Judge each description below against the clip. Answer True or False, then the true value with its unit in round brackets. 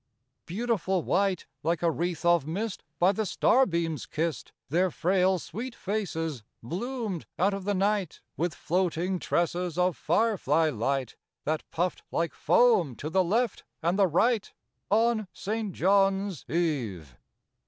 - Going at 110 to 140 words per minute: True (135 wpm)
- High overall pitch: False (180 Hz)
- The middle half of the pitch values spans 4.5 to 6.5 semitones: False (3.7 semitones)